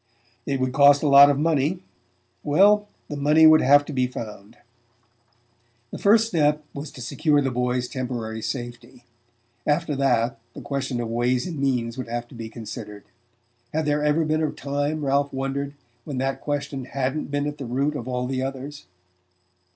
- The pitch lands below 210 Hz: Yes, low, 135 Hz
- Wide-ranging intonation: No, average, 3.1 semitones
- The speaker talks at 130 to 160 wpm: No, average, 175 wpm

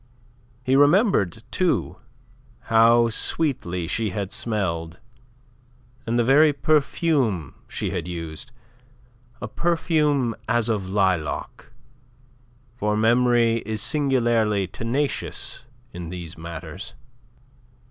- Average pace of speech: No, slow, 95 wpm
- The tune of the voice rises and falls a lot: Yes, wide, 6.5 semitones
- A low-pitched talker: Yes, low, 115 Hz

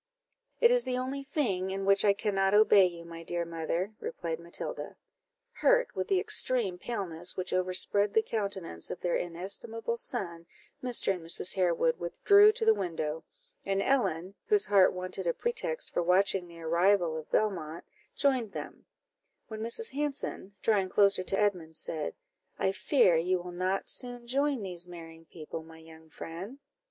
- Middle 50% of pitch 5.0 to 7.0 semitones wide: Yes, wide, 5.5 semitones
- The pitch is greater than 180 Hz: Yes, high, 190 Hz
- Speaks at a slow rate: No, average, 165 wpm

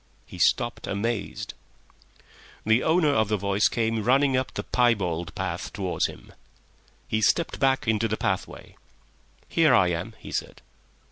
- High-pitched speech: No, low, 110 Hz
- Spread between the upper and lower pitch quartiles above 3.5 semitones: Yes, average, 4.5 semitones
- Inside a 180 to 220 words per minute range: No, average, 145 wpm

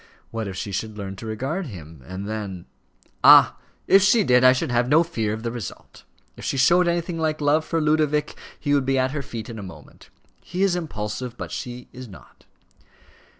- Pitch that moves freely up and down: Yes, wide, 6.2 semitones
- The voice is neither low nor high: No, low, 125 Hz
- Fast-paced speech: Yes, fast, 210 wpm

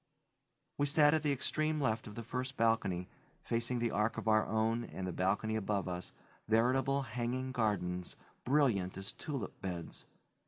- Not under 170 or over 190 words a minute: No, average, 160 wpm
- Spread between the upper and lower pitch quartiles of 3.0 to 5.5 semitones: Yes, average, 4.4 semitones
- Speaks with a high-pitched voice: No, low, 115 Hz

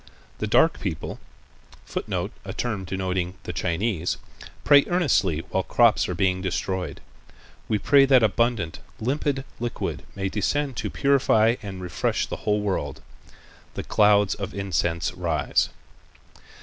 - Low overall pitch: Yes, low, 100 Hz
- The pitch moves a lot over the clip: No, average, 4.6 semitones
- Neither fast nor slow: No, slow, 130 wpm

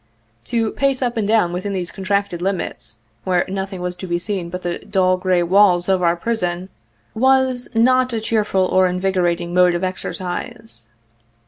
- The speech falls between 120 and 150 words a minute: No, average, 165 wpm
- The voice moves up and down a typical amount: Yes, average, 3.6 semitones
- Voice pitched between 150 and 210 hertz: Yes, high, 190 Hz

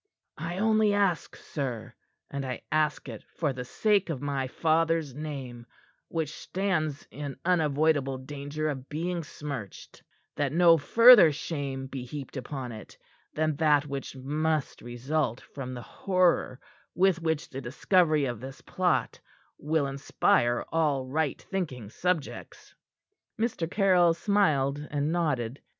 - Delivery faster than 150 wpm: No, slow, 135 wpm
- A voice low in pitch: No, medium, 150 Hz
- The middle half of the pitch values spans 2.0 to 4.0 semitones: Yes, average, 3.7 semitones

